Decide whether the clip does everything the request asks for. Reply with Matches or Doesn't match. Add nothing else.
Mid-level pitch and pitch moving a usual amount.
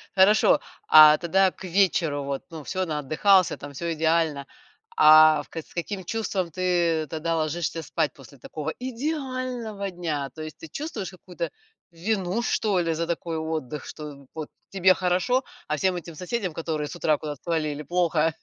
Matches